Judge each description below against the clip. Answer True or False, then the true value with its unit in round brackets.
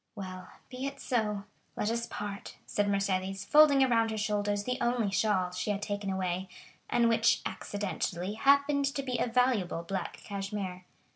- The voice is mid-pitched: False (205 Hz)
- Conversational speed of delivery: True (155 wpm)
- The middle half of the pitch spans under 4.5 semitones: True (3.7 semitones)